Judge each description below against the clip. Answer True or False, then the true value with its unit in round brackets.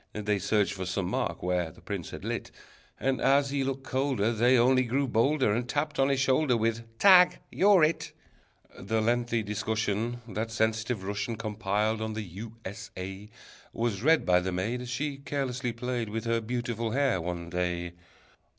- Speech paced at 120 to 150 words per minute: False (180 wpm)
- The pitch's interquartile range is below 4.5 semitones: True (4.1 semitones)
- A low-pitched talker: True (115 Hz)